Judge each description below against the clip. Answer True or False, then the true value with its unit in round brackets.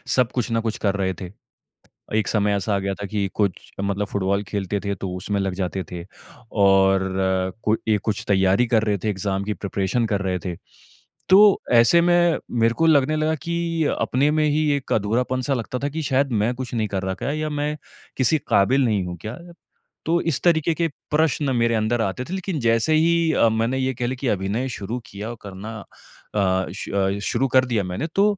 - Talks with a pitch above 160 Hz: False (115 Hz)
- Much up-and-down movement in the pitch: True (6.5 semitones)